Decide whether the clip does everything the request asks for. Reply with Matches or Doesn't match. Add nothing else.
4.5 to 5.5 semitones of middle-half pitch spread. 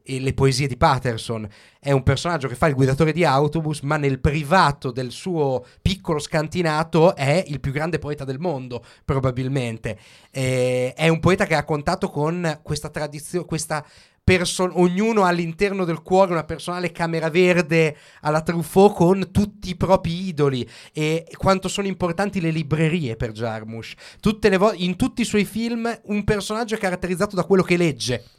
Matches